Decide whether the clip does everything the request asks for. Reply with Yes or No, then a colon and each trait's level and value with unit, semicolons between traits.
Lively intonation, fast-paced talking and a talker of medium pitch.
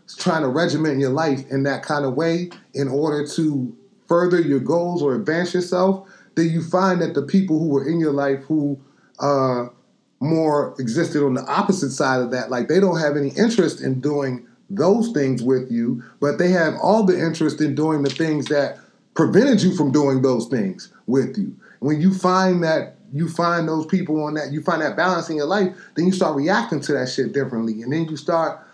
No: average, 4.2 semitones; fast, 210 wpm; medium, 155 Hz